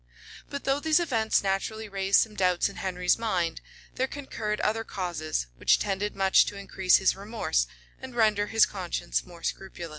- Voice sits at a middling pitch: No, high, 200 Hz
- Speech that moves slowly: No, average, 175 wpm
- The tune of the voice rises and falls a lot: No, average, 3.3 semitones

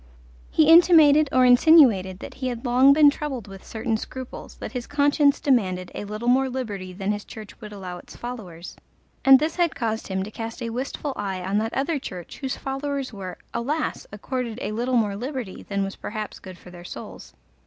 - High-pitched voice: Yes, high, 235 Hz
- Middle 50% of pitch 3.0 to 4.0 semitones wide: No, average, 5.3 semitones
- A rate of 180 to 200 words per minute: Yes, average, 195 wpm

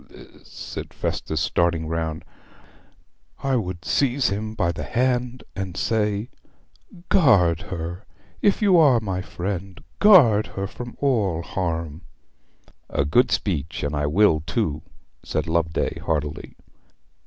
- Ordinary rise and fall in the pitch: No, wide, 6.5 semitones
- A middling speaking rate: No, slow, 125 wpm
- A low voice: Yes, very low, 95 Hz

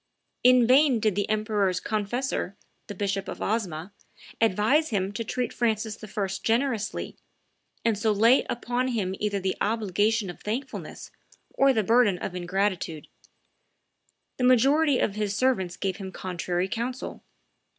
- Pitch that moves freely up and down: No, average, 3.7 semitones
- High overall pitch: Yes, high, 215 Hz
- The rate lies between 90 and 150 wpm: Yes, average, 140 wpm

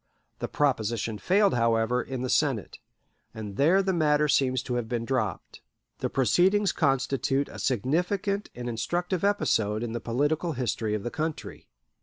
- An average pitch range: No, wide, 6.0 semitones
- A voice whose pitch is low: Yes, low, 130 Hz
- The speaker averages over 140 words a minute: Yes, average, 155 wpm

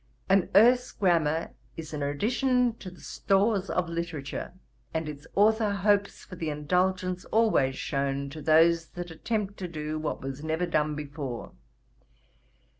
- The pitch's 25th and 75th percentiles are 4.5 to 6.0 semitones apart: Yes, average, 4.9 semitones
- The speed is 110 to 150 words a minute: Yes, average, 145 wpm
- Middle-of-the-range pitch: Yes, medium, 170 Hz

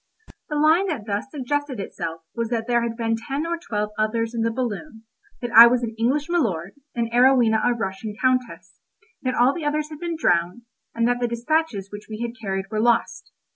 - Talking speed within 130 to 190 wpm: No, fast, 205 wpm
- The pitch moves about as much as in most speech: Yes, average, 3.7 semitones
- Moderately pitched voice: No, high, 235 Hz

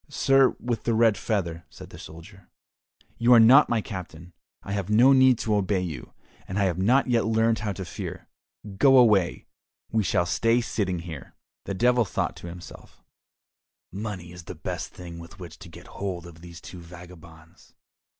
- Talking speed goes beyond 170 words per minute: Yes, average, 180 wpm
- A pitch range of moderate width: Yes, average, 4.8 semitones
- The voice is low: Yes, very low, 95 Hz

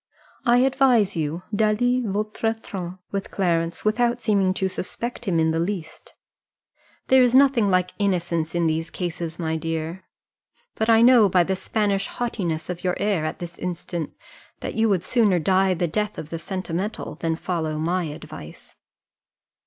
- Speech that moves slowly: No, average, 160 wpm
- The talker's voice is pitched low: No, medium, 185 Hz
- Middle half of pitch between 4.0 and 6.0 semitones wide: Yes, average, 4.3 semitones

